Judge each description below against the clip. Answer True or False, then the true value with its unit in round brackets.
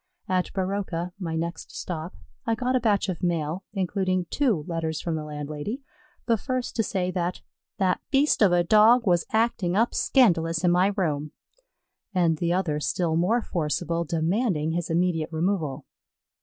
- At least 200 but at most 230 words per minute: False (160 wpm)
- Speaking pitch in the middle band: True (180 Hz)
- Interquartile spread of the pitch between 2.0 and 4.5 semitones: True (3.8 semitones)